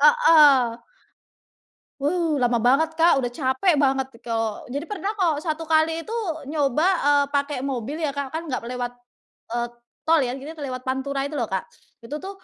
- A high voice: Yes, very high, 280 Hz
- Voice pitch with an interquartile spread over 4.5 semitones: No, average, 3.8 semitones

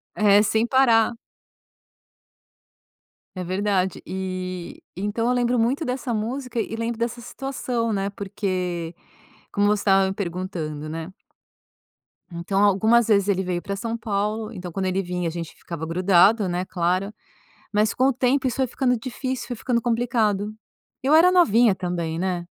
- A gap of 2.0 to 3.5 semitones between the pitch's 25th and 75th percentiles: No, average, 4.3 semitones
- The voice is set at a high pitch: Yes, high, 205 Hz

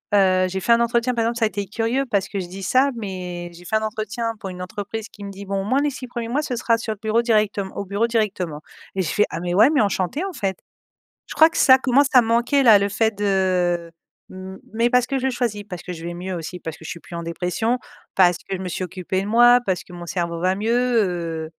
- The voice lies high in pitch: Yes, high, 205 Hz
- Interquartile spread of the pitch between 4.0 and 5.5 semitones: Yes, average, 4.3 semitones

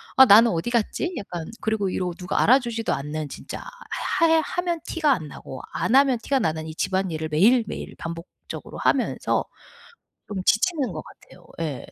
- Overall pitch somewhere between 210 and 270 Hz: Yes, high, 220 Hz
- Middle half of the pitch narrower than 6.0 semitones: No, wide, 8.3 semitones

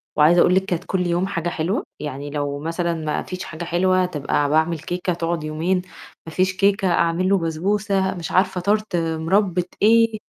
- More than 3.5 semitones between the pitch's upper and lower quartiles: No, average, 2.8 semitones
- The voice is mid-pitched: Yes, medium, 175 Hz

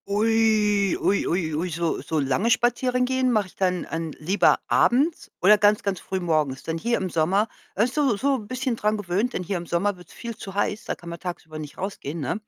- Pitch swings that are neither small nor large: Yes, average, 4.8 semitones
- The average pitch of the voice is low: No, high, 200 Hz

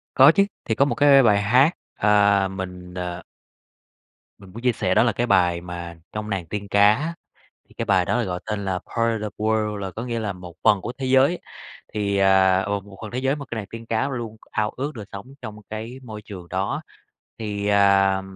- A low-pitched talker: Yes, low, 105 Hz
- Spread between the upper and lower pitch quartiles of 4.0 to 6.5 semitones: No, average, 3.3 semitones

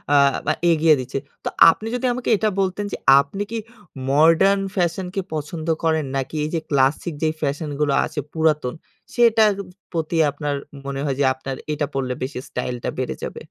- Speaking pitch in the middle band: Yes, medium, 155 Hz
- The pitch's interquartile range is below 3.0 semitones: No, average, 4.2 semitones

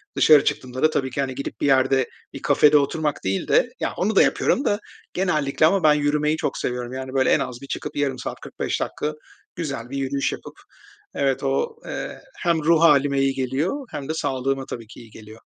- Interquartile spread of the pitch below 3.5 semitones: Yes, average, 2.7 semitones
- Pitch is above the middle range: No, medium, 140 Hz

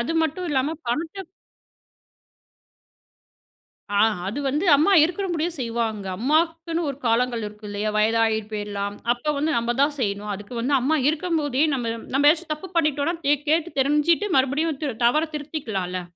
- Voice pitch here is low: No, very high, 280 Hz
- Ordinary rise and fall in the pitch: No, wide, 5.7 semitones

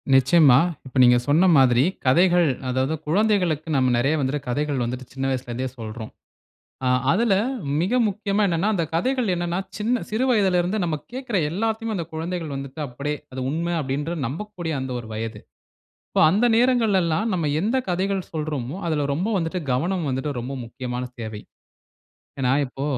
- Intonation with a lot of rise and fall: Yes, wide, 6.5 semitones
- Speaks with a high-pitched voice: No, medium, 160 Hz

